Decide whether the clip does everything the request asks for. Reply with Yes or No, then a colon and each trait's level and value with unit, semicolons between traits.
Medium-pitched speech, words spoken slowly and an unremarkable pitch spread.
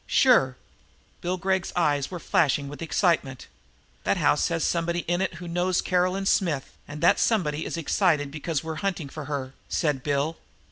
No: medium, 165 Hz; average, 175 wpm; average, 3.6 semitones